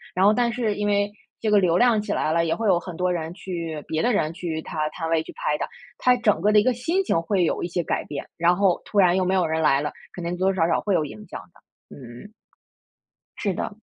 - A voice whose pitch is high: No, medium, 180 Hz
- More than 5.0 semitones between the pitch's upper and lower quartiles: No, average, 4.2 semitones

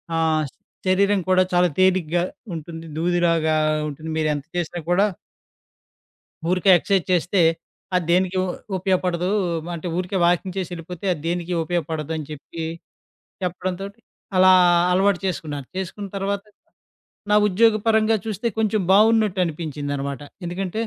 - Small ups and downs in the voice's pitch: No, average, 3.0 semitones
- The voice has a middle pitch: Yes, medium, 180 Hz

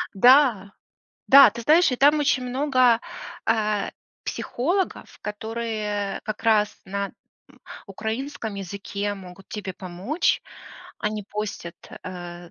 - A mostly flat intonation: No, average, 4.2 semitones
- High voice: Yes, high, 215 Hz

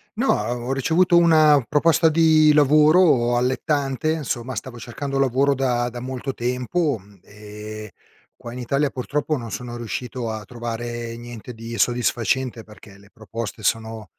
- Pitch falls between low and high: No, low, 125 Hz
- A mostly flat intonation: No, average, 3.7 semitones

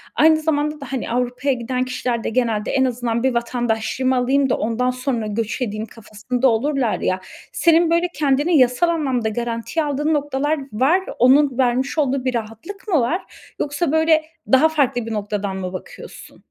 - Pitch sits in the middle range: No, very high, 255 Hz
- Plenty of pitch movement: No, average, 4.0 semitones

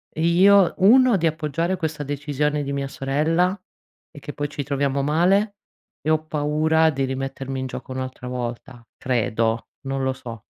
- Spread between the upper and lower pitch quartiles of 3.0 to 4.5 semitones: Yes, average, 3.3 semitones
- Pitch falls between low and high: Yes, medium, 145 Hz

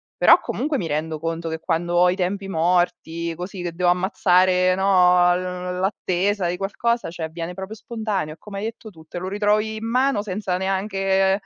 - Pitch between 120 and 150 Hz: No, medium, 185 Hz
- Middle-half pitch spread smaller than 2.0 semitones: No, narrow, 2.4 semitones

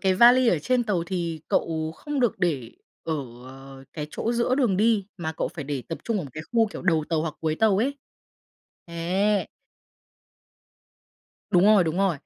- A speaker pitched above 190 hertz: No, medium, 185 Hz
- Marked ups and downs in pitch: Yes, wide, 5.7 semitones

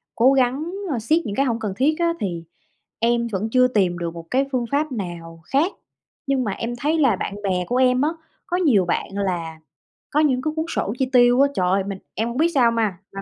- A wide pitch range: Yes, wide, 5.8 semitones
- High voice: Yes, high, 235 Hz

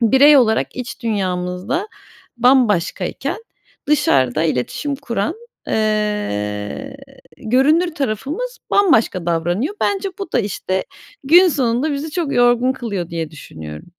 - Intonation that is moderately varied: No, wide, 7.9 semitones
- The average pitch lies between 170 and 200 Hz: No, high, 235 Hz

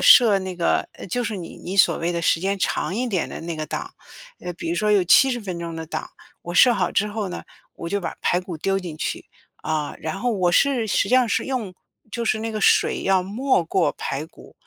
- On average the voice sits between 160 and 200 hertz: Yes, high, 190 Hz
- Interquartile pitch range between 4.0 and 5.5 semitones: Yes, average, 4.3 semitones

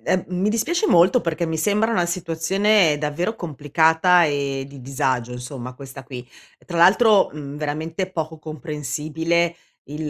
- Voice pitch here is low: No, medium, 160 Hz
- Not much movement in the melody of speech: No, average, 3.8 semitones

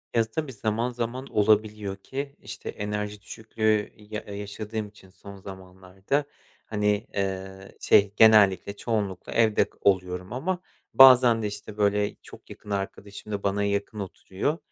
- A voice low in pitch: Yes, low, 105 Hz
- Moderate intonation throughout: No, narrow, 2.0 semitones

